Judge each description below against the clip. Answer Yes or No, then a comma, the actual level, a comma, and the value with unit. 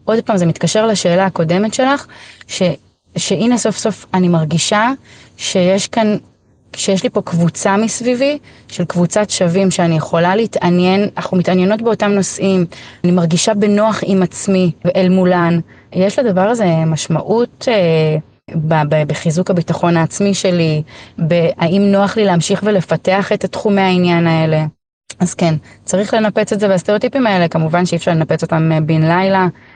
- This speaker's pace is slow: No, average, 145 wpm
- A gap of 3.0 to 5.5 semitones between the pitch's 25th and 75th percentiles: Yes, average, 3.7 semitones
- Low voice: No, medium, 180 Hz